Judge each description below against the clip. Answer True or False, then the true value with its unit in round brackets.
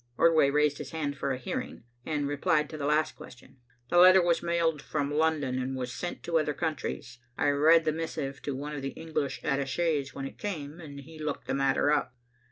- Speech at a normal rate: False (210 wpm)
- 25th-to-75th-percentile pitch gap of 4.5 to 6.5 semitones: False (2.7 semitones)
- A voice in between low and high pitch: True (150 Hz)